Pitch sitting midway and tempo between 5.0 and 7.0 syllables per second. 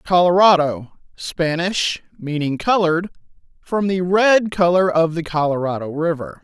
No: medium, 170 Hz; 4.5 syllables/s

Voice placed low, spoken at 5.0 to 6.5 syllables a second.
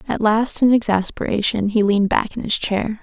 No: high, 215 Hz; 5.2 syllables/s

